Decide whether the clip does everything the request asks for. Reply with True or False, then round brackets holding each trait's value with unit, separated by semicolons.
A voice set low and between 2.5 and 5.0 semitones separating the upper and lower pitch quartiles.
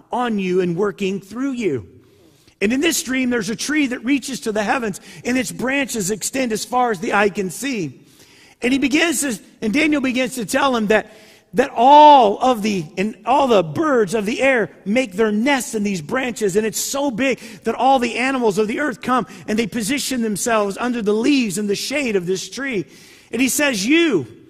False (235 Hz; 3.9 semitones)